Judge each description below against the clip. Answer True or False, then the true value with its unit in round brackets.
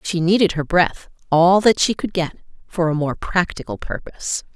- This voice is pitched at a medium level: True (175 Hz)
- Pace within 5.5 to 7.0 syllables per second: False (4.9 syllables/s)